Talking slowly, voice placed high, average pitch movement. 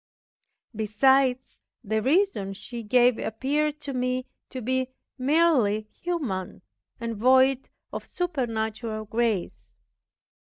Yes: slow, 95 wpm; very high, 250 Hz; average, 3.7 semitones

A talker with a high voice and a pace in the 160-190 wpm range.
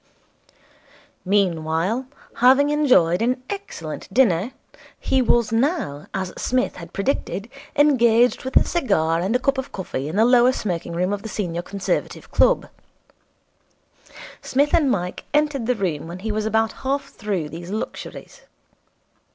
No: high, 220 Hz; average, 145 wpm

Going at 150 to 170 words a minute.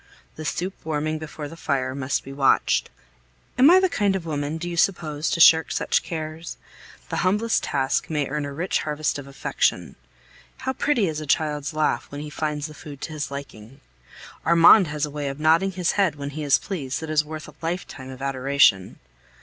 No: average, 200 wpm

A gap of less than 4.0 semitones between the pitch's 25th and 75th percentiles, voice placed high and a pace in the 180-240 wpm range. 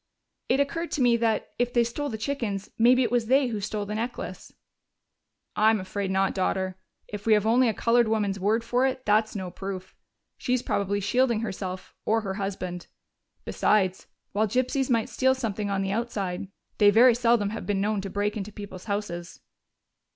Yes: average, 3.3 semitones; high, 215 Hz; average, 185 wpm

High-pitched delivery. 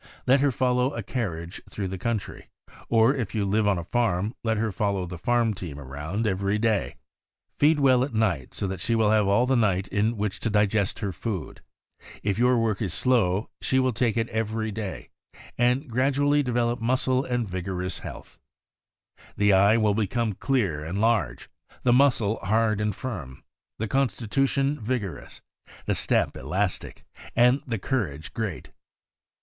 No: low, 110 Hz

